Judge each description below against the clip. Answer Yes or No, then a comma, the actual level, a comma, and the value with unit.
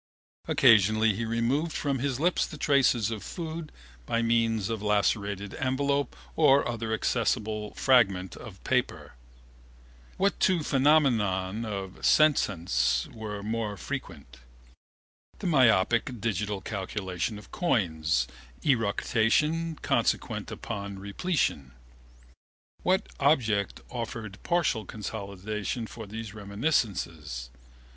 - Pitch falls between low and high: No, low, 110 Hz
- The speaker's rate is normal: No, slow, 105 wpm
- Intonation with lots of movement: No, average, 4.9 semitones